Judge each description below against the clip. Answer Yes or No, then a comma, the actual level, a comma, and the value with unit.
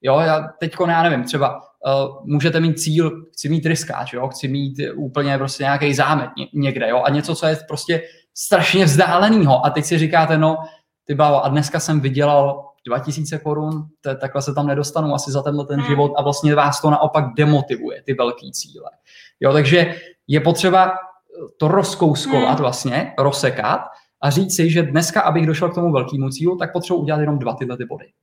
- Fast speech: Yes, fast, 185 wpm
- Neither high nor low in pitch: Yes, medium, 150 Hz